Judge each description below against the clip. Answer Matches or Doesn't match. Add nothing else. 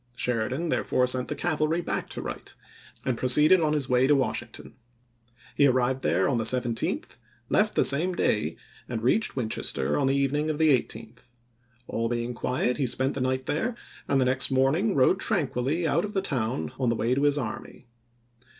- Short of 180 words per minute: Doesn't match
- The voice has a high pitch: Doesn't match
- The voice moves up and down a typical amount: Matches